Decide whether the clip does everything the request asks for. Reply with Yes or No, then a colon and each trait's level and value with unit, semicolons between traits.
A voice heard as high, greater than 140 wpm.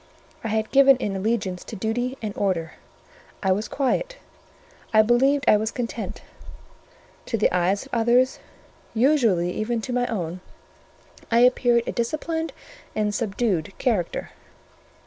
No: high, 225 Hz; slow, 135 wpm